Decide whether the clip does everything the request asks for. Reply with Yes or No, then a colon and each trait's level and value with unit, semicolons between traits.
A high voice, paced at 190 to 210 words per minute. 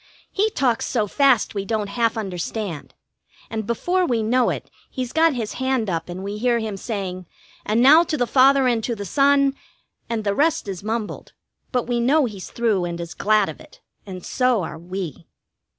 Yes: high, 225 Hz; average, 200 wpm